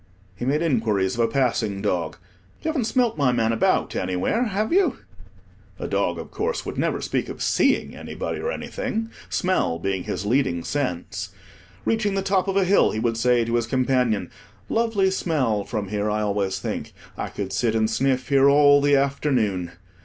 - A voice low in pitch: Yes, low, 125 Hz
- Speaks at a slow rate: No, average, 180 wpm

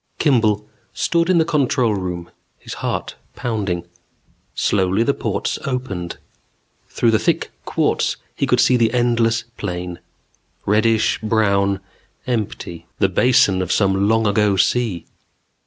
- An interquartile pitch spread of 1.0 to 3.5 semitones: No, average, 3.9 semitones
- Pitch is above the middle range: No, low, 110 Hz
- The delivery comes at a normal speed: No, slow, 125 wpm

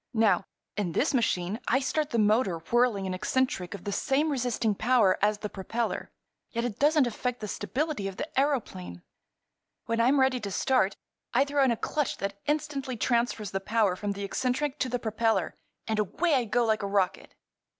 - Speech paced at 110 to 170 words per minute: No, average, 185 wpm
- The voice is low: No, high, 230 Hz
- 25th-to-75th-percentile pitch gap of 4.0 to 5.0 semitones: Yes, average, 4.5 semitones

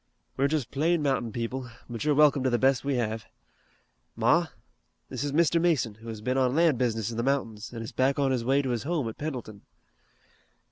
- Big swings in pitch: No, average, 3.6 semitones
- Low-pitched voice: Yes, low, 130 Hz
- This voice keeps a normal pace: No, fast, 215 wpm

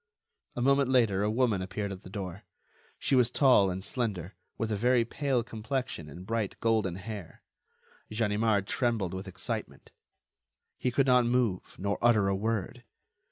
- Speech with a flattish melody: No, average, 3.8 semitones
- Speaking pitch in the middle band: No, low, 110 Hz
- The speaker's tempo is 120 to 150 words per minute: No, average, 160 wpm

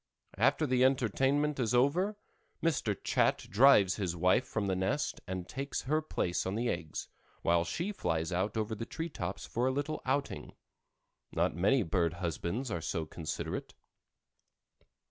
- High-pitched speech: No, low, 110 Hz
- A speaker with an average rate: Yes, average, 155 wpm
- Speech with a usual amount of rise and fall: No, wide, 7.3 semitones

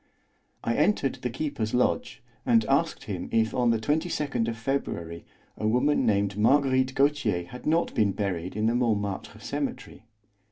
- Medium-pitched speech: No, low, 115 Hz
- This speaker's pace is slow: No, average, 155 wpm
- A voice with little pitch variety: No, average, 4.6 semitones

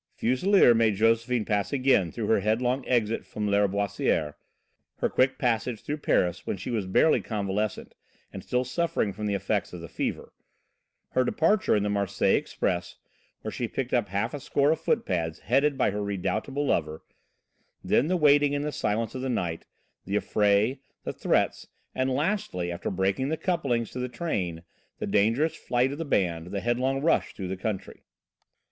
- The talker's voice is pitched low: Yes, low, 115 Hz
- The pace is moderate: Yes, average, 175 wpm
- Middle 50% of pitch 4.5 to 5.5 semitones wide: Yes, average, 5.2 semitones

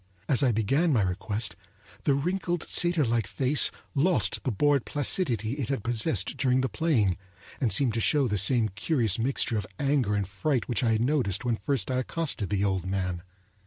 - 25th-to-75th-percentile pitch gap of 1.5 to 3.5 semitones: No, average, 5.3 semitones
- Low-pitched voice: Yes, low, 120 Hz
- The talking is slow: No, average, 185 wpm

